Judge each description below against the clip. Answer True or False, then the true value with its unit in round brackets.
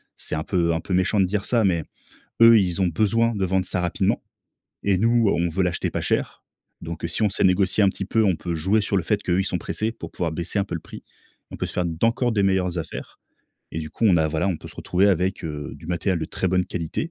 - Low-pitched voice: True (95 Hz)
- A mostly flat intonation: False (3.1 semitones)